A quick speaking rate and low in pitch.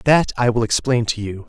Yes: fast, 245 wpm; low, 115 Hz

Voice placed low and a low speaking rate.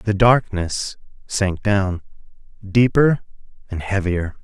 Yes: low, 100 Hz; slow, 95 wpm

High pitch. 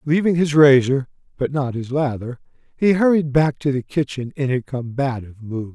No: low, 135 Hz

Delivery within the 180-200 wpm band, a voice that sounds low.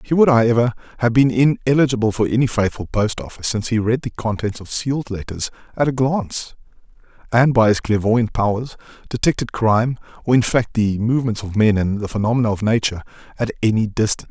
Yes: average, 185 wpm; low, 115 Hz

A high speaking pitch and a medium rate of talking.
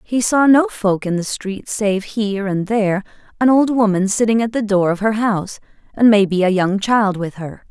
No: high, 210 Hz; fast, 220 wpm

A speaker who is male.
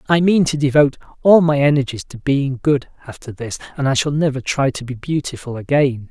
Yes: male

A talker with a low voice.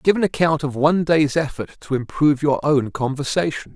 No: medium, 150 Hz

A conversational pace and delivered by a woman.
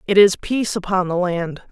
No: fast, 210 wpm; female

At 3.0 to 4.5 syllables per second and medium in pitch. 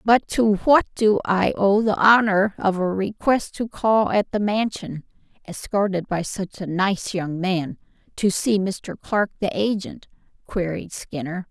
No: 3.9 syllables/s; high, 200 Hz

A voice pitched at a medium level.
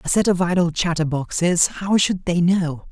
Yes: medium, 175 Hz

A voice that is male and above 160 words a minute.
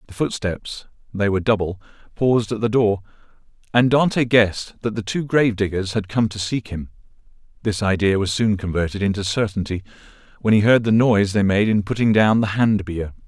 Yes: male; average, 170 wpm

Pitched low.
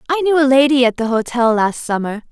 No: high, 245 Hz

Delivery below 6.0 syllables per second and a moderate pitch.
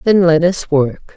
Yes: 3.9 syllables/s; medium, 165 Hz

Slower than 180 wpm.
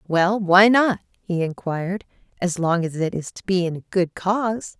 No: average, 200 wpm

